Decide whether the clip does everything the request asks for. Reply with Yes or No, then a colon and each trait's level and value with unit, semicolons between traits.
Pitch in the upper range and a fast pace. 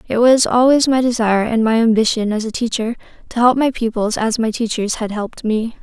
Yes: high, 230 Hz; fast, 215 wpm